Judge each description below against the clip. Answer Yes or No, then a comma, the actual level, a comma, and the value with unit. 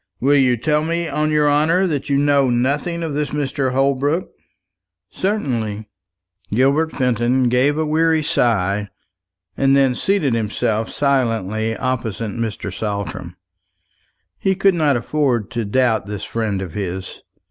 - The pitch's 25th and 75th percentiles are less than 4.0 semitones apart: No, average, 5.0 semitones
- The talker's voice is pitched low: Yes, low, 130 Hz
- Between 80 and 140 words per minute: Yes, slow, 135 wpm